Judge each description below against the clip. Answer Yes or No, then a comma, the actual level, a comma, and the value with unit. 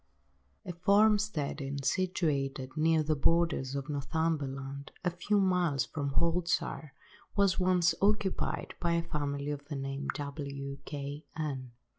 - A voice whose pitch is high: No, medium, 150 Hz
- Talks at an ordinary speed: No, slow, 130 wpm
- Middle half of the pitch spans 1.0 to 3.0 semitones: No, average, 3.9 semitones